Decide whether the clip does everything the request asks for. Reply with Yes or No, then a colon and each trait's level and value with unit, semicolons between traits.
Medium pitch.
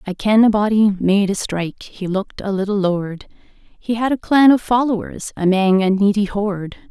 No: high, 205 Hz